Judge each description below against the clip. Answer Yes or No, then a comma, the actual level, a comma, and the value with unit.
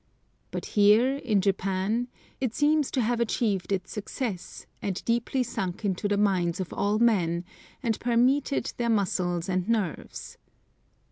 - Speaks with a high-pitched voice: Yes, high, 210 Hz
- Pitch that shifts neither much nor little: Yes, average, 4.1 semitones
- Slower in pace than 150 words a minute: Yes, average, 140 wpm